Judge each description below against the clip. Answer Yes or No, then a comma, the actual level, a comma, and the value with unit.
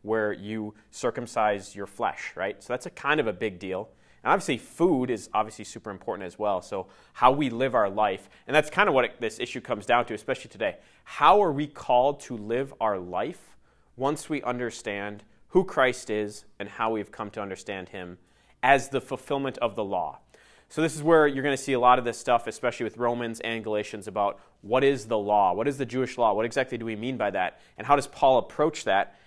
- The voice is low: Yes, low, 115 Hz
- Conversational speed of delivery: No, fast, 225 wpm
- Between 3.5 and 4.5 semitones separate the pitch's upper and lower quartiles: Yes, average, 3.9 semitones